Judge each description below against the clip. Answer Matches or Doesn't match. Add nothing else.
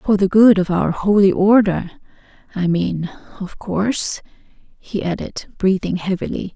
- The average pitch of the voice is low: Doesn't match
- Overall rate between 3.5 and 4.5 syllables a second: Matches